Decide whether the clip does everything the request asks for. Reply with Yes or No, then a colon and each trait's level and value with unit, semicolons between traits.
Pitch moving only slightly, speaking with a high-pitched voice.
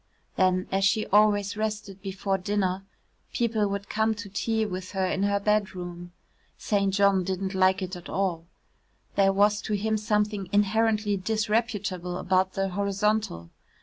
Yes: narrow, 1.9 semitones; high, 200 Hz